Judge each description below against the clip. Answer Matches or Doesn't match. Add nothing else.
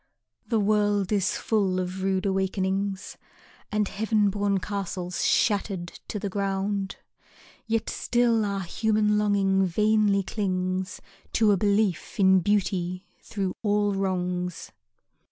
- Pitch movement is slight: Matches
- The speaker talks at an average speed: Doesn't match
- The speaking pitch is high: Matches